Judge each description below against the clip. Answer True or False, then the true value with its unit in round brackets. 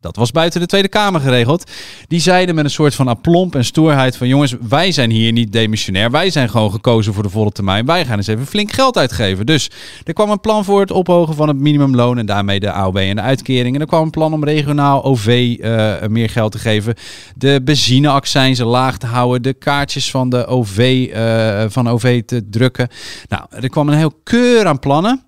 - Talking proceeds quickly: True (220 wpm)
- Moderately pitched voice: False (130 Hz)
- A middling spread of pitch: True (4.9 semitones)